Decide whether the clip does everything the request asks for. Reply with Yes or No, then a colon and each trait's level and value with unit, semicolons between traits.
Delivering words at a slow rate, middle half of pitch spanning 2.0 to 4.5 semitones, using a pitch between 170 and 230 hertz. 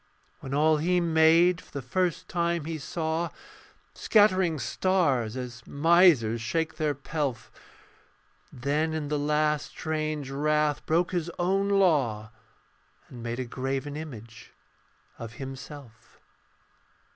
No: slow, 120 wpm; average, 4.1 semitones; medium, 150 Hz